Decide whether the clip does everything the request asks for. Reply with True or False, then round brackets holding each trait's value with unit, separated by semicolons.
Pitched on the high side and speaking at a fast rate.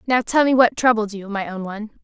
True (220 Hz; 265 wpm)